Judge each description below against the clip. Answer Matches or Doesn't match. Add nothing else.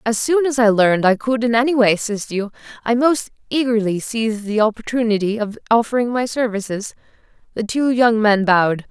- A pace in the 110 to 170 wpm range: Doesn't match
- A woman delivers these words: Matches